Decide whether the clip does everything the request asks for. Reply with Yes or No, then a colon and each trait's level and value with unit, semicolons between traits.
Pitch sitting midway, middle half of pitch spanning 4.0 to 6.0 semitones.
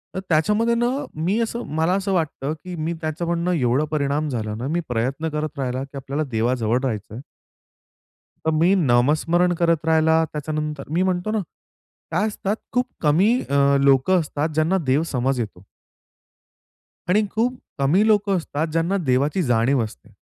Yes: medium, 155 Hz; average, 4.9 semitones